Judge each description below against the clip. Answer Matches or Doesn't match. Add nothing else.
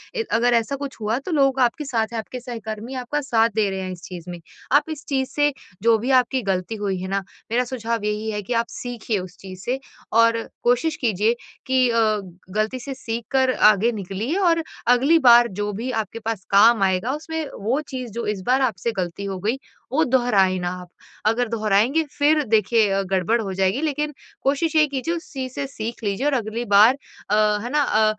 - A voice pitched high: Matches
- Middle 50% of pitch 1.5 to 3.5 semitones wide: Doesn't match